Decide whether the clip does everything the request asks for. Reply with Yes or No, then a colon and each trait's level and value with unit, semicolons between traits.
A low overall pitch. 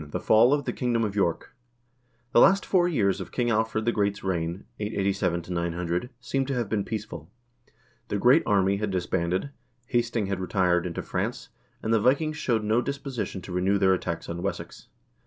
Yes: low, 105 Hz